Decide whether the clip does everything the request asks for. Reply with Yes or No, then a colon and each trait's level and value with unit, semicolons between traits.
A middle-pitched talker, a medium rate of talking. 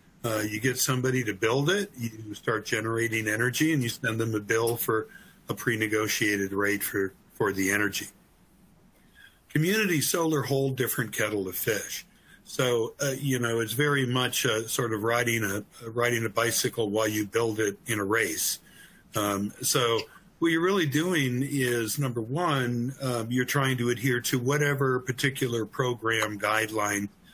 No: low, 120 Hz; average, 160 wpm